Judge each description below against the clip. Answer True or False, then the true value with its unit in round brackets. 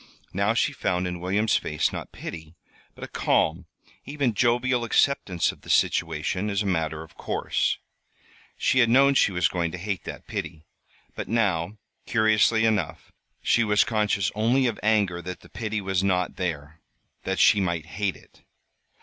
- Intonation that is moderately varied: True (4.2 semitones)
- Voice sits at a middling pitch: False (100 Hz)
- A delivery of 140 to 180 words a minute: True (165 wpm)